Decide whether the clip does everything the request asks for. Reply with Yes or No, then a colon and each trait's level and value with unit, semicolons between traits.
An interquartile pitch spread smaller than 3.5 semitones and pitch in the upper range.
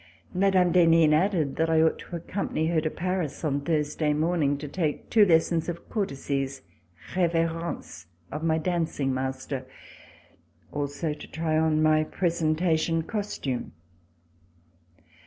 No: narrow, 2.5 semitones; medium, 160 Hz